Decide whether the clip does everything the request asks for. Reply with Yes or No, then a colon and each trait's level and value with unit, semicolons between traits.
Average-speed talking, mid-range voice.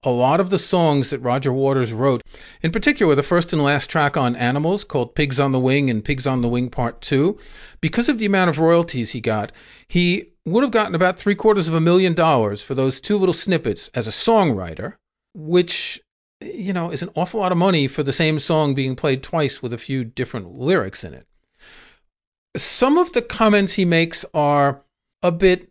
No: fast, 210 wpm; medium, 155 Hz